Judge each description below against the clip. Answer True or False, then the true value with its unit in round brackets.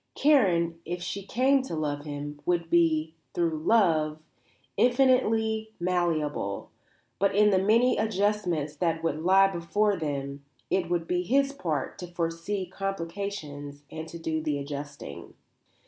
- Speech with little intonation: False (4.7 semitones)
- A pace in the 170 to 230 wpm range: False (135 wpm)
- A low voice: False (170 Hz)